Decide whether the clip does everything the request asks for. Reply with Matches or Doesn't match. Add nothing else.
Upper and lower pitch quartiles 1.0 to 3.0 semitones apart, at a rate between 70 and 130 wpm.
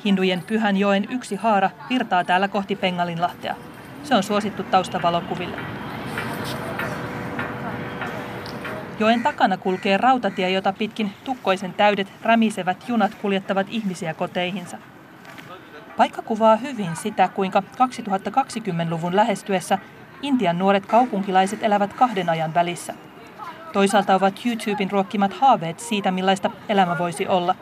Matches